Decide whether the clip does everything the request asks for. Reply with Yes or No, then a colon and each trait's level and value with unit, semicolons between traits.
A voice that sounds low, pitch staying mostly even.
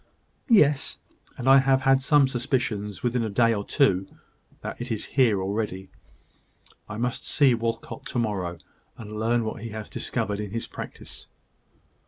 No: low, 115 Hz; average, 3.9 semitones